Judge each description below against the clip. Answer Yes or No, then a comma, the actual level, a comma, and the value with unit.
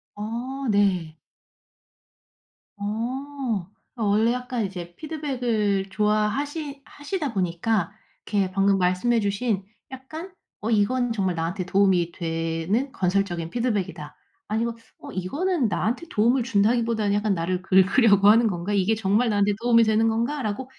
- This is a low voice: No, high, 210 Hz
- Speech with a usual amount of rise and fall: Yes, average, 4.1 semitones